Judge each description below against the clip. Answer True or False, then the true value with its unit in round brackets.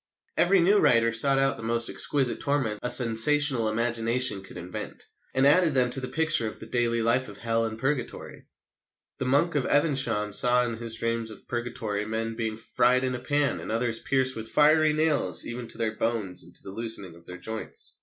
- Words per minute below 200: False (205 wpm)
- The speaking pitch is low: True (120 Hz)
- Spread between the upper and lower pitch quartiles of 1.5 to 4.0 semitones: True (3.3 semitones)